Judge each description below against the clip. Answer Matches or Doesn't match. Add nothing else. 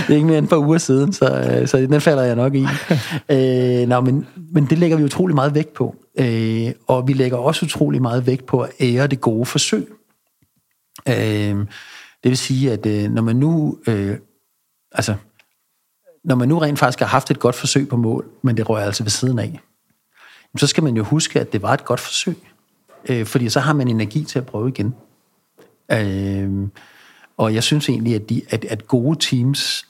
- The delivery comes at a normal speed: Matches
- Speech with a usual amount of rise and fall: Matches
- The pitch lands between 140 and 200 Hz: Doesn't match